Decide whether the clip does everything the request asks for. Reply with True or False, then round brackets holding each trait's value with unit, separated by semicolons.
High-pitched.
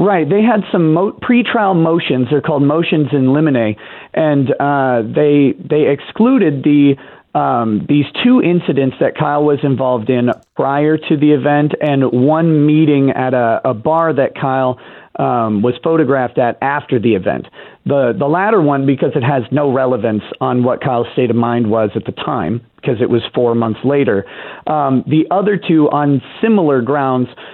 False (140 Hz)